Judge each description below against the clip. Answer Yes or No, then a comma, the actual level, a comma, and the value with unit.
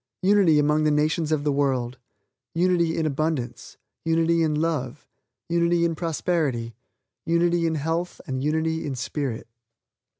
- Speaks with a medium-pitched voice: Yes, medium, 160 Hz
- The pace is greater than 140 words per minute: No, slow, 135 wpm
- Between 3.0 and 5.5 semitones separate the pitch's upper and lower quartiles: No, narrow, 2.6 semitones